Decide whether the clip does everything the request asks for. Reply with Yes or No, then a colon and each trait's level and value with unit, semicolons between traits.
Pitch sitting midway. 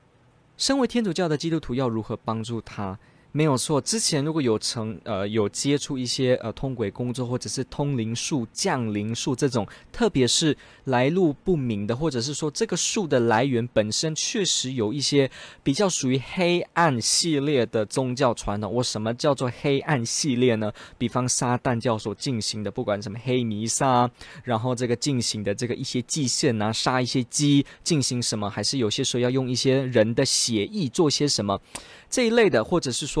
No: low, 125 Hz